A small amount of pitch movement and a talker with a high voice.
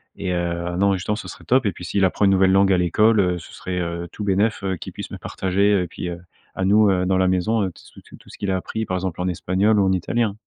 No: narrow, 2.1 semitones; very low, 95 Hz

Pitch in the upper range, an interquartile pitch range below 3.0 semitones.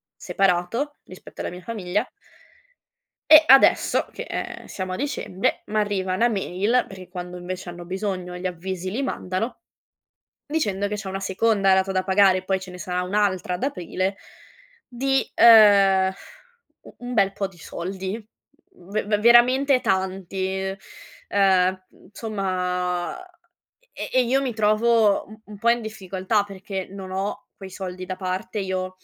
Yes: high, 195 Hz; narrow, 2.6 semitones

